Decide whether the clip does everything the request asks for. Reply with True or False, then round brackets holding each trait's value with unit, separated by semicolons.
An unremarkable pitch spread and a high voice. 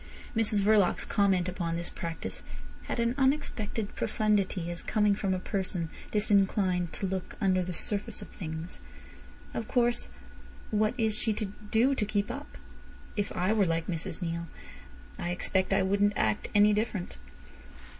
True (3.0 semitones; 200 Hz)